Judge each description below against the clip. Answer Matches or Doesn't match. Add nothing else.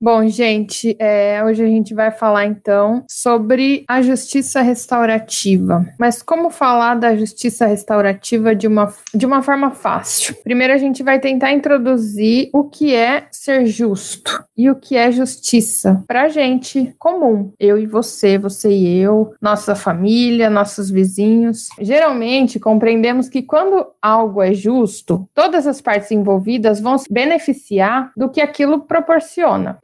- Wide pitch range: Doesn't match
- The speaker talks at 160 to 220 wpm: Doesn't match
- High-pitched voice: Matches